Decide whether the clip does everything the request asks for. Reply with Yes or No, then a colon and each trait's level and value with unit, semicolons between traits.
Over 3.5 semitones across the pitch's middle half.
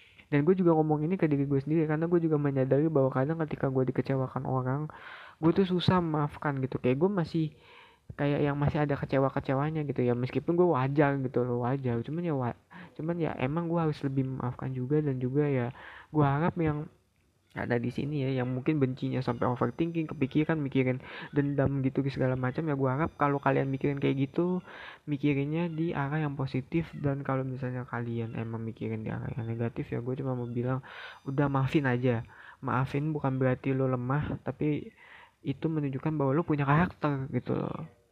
No: average, 3.1 semitones